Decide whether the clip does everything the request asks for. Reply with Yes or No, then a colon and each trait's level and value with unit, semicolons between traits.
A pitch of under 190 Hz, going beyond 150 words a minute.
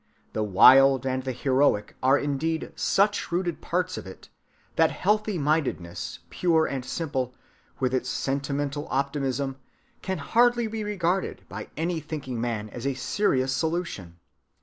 No: medium, 140 Hz; slow, 135 wpm